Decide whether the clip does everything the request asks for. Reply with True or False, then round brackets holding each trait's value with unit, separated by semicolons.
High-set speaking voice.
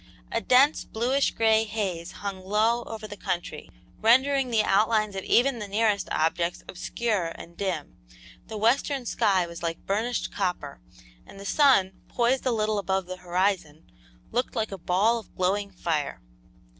True (205 Hz)